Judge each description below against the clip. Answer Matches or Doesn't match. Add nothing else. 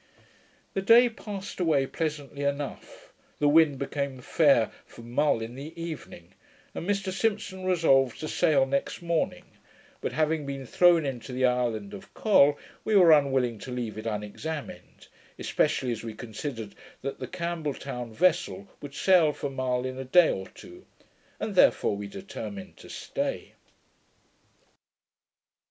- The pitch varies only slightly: Doesn't match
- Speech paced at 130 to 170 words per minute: Matches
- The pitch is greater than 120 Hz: Matches